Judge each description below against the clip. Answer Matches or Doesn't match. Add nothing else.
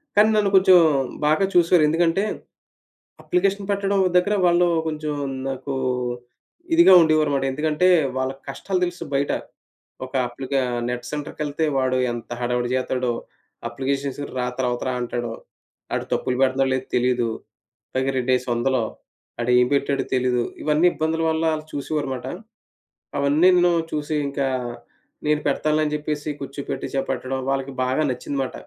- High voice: Doesn't match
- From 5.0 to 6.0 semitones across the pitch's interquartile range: Doesn't match